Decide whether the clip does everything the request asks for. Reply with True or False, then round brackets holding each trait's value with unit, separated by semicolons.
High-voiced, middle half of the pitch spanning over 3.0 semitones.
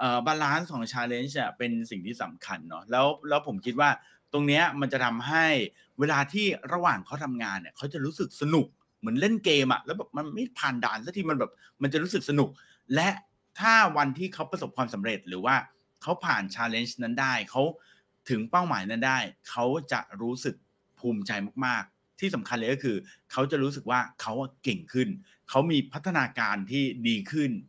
False (140 Hz; 5.0 semitones)